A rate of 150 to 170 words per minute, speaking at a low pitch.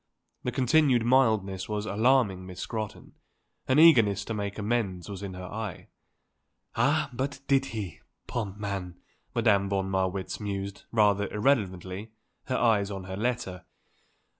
No: average, 140 wpm; low, 105 Hz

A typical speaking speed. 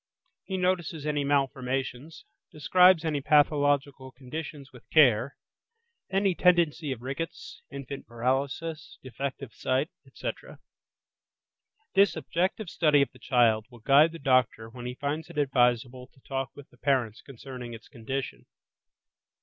No: slow, 130 wpm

